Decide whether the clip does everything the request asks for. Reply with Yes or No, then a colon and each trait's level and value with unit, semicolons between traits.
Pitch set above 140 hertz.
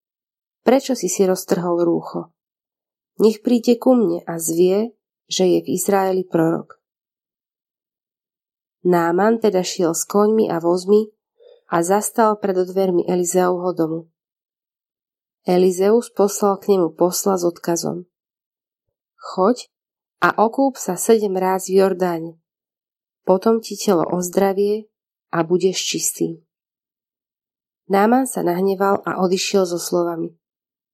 Yes: high, 190 Hz